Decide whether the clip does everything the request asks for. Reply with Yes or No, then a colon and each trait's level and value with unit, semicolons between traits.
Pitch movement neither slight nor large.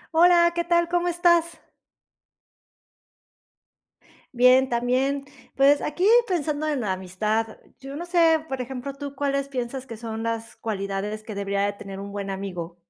No: wide, 6.5 semitones